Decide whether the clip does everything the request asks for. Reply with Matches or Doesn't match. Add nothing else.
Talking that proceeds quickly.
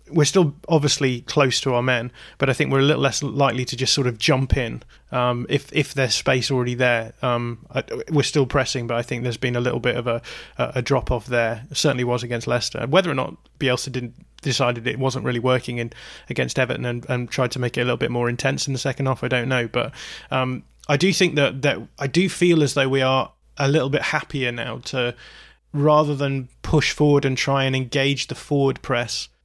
Matches